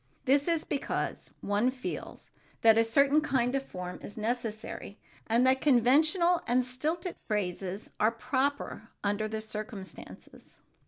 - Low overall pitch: No, high, 245 Hz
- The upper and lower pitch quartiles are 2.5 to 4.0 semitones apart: No, average, 4.4 semitones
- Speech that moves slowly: Yes, slow, 130 wpm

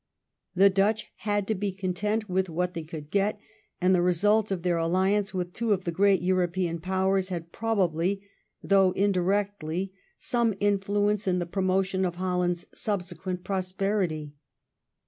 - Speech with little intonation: Yes, narrow, 2.1 semitones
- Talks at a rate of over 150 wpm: No, average, 145 wpm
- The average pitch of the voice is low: No, high, 190 Hz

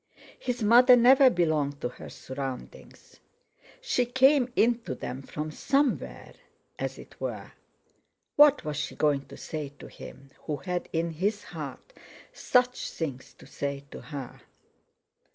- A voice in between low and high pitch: Yes, medium, 170 Hz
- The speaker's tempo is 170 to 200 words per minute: No, slow, 135 wpm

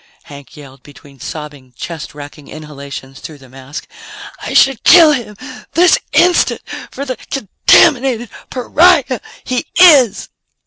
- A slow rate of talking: Yes, slow, 125 wpm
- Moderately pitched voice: Yes, medium, 175 Hz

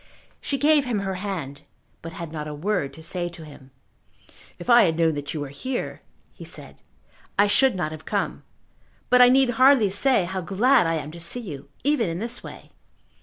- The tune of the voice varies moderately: No, wide, 7.4 semitones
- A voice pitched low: No, medium, 185 Hz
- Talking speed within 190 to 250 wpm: Yes, fast, 205 wpm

